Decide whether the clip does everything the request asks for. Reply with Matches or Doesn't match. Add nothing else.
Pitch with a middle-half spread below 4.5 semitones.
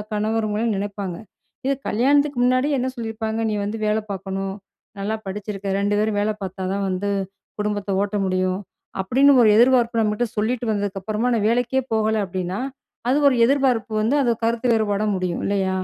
Matches